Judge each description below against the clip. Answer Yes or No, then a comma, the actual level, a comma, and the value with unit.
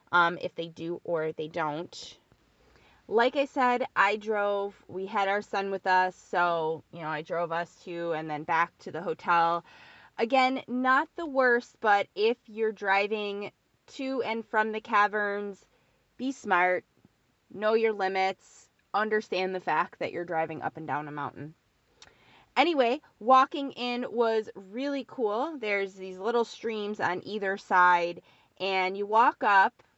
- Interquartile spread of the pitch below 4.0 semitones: No, average, 4.8 semitones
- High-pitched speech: Yes, high, 205 Hz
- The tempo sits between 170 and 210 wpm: No, average, 155 wpm